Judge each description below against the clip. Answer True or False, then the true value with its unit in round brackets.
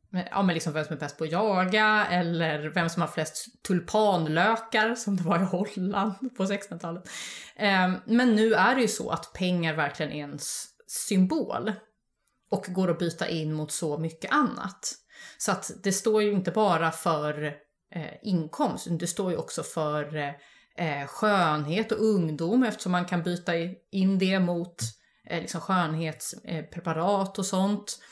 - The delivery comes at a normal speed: True (150 wpm)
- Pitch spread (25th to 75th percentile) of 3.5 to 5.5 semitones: True (3.9 semitones)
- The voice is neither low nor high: True (180 Hz)